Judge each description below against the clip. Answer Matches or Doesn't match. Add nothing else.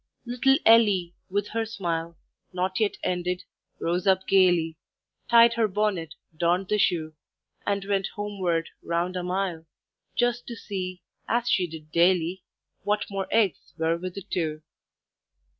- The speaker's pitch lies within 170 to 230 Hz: Matches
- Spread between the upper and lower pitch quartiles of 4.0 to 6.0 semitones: Doesn't match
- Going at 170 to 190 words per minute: Doesn't match